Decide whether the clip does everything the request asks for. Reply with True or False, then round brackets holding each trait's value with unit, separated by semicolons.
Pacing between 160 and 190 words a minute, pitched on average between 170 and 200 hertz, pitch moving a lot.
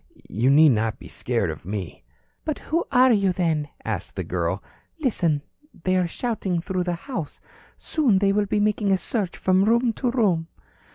True (180 wpm; 185 Hz; 6.8 semitones)